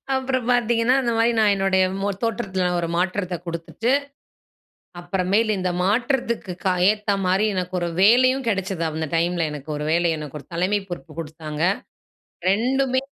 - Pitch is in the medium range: No, high, 195 Hz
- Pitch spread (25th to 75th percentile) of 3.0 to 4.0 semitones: No, average, 4.9 semitones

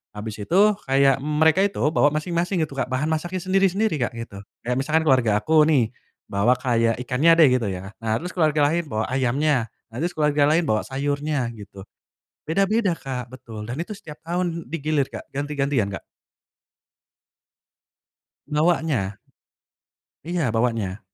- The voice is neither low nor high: Yes, medium, 145 Hz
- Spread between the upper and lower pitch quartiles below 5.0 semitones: No, average, 5.3 semitones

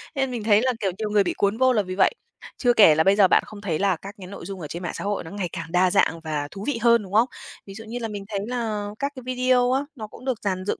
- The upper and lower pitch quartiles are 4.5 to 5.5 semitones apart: No, average, 4.0 semitones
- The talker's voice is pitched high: Yes, high, 205 Hz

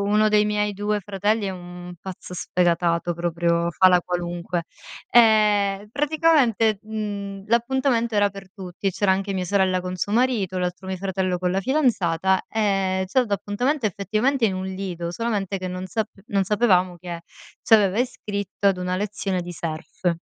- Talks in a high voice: Yes, high, 195 Hz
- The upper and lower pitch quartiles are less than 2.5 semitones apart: No, average, 2.8 semitones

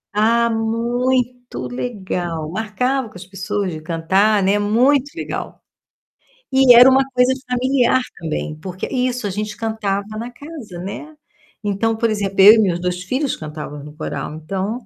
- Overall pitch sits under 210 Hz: No, high, 215 Hz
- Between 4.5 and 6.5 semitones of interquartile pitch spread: Yes, average, 4.9 semitones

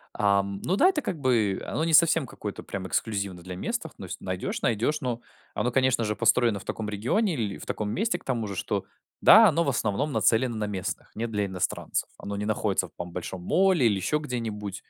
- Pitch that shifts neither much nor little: No, wide, 5.9 semitones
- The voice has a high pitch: No, low, 110 Hz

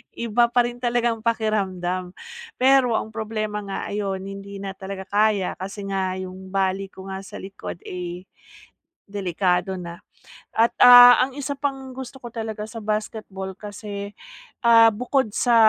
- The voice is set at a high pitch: Yes, high, 210 Hz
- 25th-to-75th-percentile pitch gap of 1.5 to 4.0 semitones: Yes, average, 3.5 semitones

